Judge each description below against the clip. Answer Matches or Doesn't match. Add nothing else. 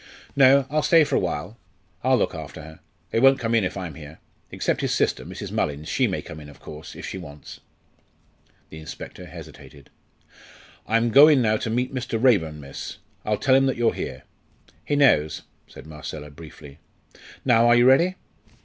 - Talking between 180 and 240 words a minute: Matches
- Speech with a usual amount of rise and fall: Doesn't match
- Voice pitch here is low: Matches